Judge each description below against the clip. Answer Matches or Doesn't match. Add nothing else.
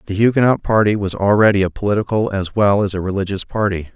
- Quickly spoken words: Doesn't match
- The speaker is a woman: Doesn't match